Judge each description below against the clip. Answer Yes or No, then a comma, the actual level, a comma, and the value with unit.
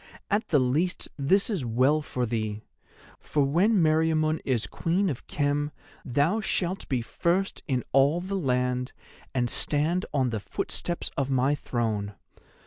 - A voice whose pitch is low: No, medium, 145 Hz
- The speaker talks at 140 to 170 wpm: Yes, average, 145 wpm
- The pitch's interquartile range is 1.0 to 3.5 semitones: No, average, 5.2 semitones